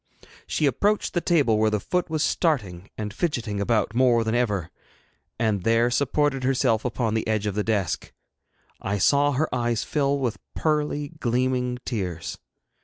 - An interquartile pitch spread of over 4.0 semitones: Yes, average, 4.8 semitones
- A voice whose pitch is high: No, low, 120 Hz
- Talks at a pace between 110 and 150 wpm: No, average, 160 wpm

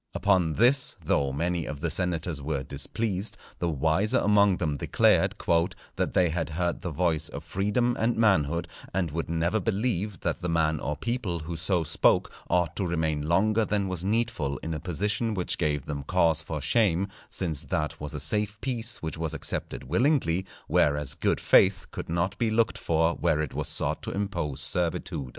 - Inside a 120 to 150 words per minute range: No, average, 185 wpm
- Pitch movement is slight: No, average, 4.6 semitones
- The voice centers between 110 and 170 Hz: No, very low, 85 Hz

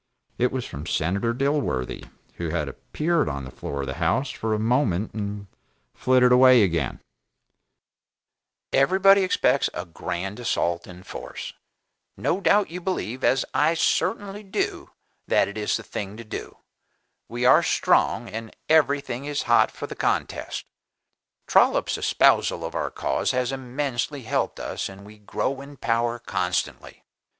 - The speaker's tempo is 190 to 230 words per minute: No, average, 150 wpm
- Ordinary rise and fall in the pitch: No, wide, 6.3 semitones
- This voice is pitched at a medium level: No, low, 120 Hz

